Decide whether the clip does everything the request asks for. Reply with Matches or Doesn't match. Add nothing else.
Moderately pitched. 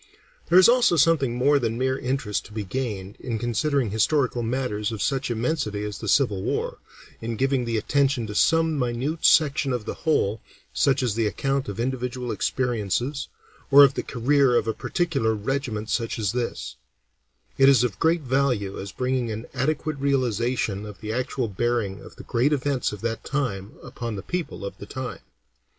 Doesn't match